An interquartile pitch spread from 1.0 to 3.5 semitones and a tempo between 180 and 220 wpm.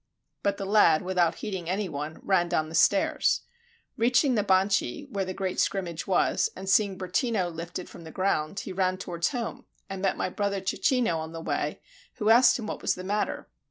Yes: average, 2.9 semitones; average, 195 wpm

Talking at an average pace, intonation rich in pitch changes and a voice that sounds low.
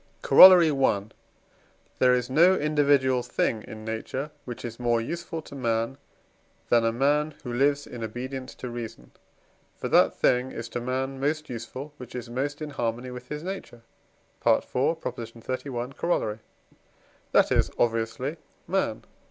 No: average, 145 wpm; average, 3.6 semitones; low, 130 Hz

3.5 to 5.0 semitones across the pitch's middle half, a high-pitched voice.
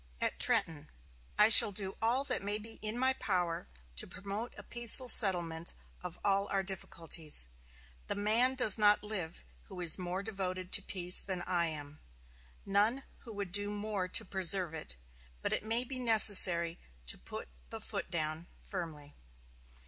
Yes: average, 4.0 semitones; high, 195 Hz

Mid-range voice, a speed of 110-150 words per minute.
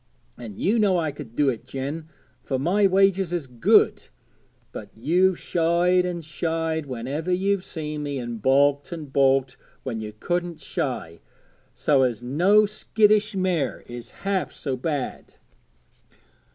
Yes: medium, 155 Hz; average, 140 wpm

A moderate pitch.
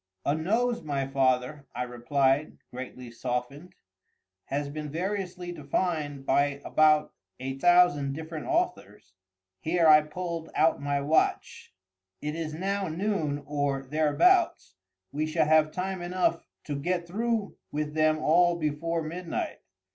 Yes: medium, 155 Hz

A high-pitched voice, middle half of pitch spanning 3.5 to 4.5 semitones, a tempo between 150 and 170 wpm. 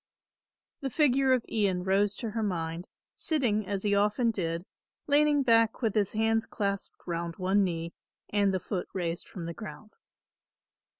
Yes: high, 205 Hz; average, 3.8 semitones; average, 160 wpm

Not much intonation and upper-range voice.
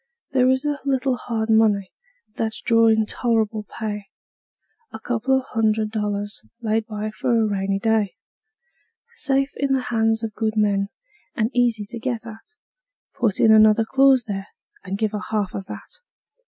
Yes: narrow, 2.3 semitones; high, 220 Hz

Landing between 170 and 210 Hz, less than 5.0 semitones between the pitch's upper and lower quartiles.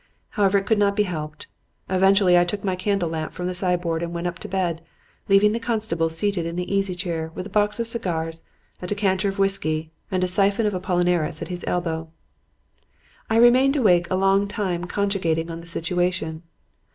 Yes: medium, 185 Hz; average, 2.9 semitones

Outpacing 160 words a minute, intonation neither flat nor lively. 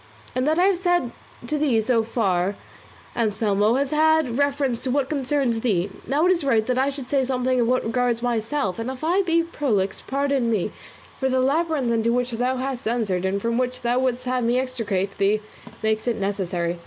Yes: fast, 205 wpm; average, 3.9 semitones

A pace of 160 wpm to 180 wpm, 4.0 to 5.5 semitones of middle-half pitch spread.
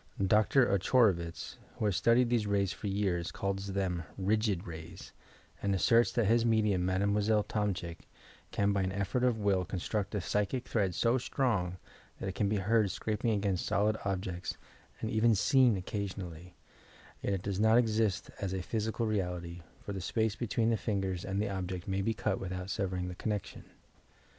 No: average, 175 wpm; average, 2.8 semitones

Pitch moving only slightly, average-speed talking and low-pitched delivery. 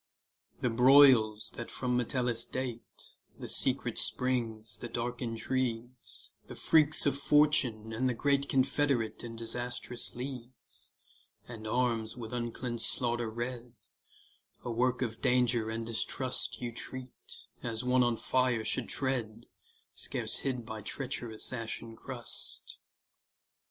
No: narrow, 2.0 semitones; slow, 125 wpm; low, 120 Hz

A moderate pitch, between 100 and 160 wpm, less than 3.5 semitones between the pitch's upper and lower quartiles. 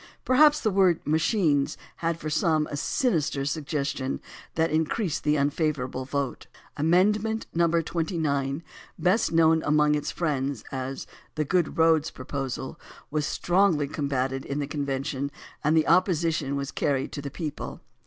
Yes: medium, 150 Hz; average, 140 wpm; average, 3.0 semitones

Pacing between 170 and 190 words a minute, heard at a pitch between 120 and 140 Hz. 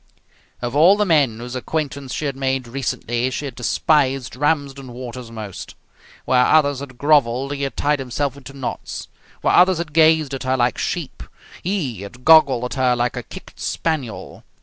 Yes: average, 175 wpm; low, 135 Hz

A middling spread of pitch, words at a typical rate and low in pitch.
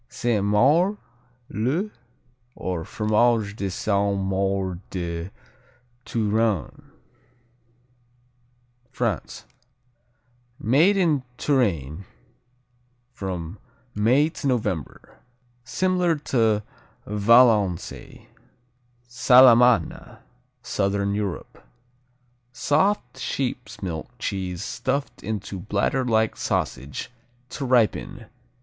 No: average, 4.6 semitones; slow, 70 wpm; low, 110 Hz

